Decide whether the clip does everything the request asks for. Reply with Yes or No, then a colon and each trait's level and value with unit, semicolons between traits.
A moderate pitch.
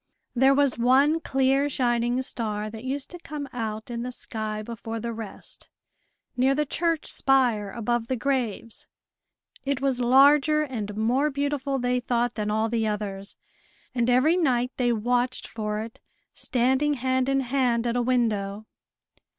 No: high, 245 Hz